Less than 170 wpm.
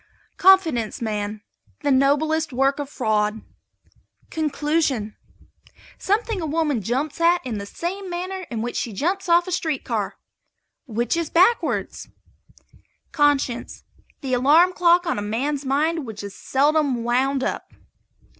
Yes: slow, 135 wpm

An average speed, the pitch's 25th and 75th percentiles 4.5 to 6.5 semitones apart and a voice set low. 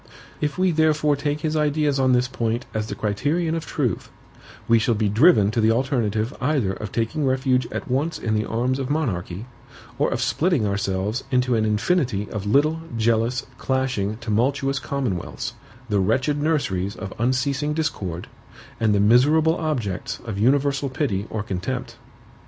Yes: average, 160 wpm; average, 5.2 semitones; low, 125 Hz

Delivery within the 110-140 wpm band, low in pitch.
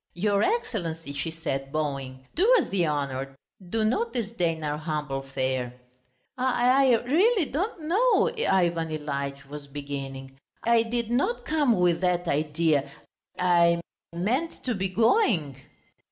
No: slow, 135 wpm; medium, 170 Hz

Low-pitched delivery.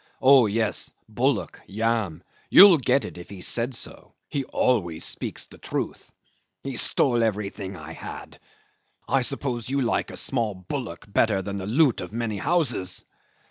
Yes: low, 115 Hz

